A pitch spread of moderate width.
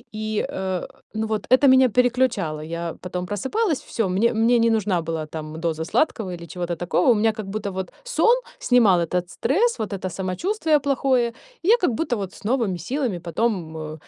No: wide, 6.0 semitones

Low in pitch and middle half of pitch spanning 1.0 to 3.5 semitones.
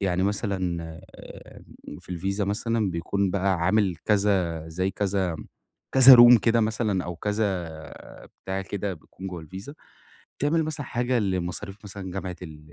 Yes: very low, 95 Hz; average, 2.8 semitones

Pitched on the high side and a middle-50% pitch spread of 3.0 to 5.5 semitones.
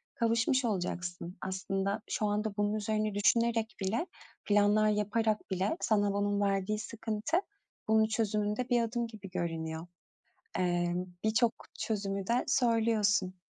No: high, 210 Hz; narrow, 2.5 semitones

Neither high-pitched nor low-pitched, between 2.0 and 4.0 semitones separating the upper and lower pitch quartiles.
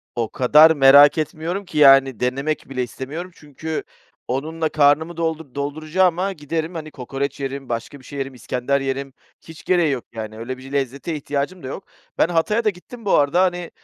Yes: medium, 145 Hz; average, 3.4 semitones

